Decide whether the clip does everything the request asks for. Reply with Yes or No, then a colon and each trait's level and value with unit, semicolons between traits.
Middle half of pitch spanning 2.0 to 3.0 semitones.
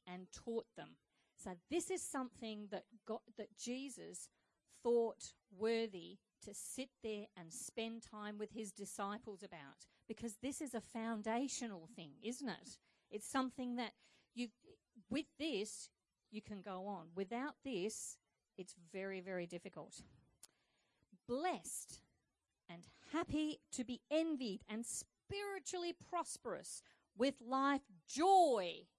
No: average, 4.7 semitones